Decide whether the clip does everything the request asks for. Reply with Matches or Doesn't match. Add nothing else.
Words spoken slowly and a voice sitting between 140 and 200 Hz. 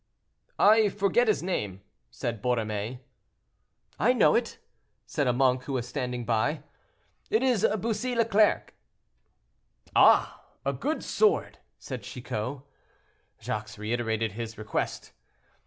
Doesn't match